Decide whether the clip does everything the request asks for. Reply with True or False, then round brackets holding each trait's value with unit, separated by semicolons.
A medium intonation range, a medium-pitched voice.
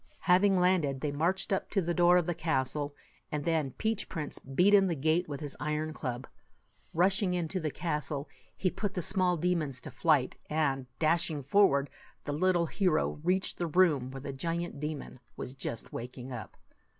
True (4.1 semitones; 160 Hz)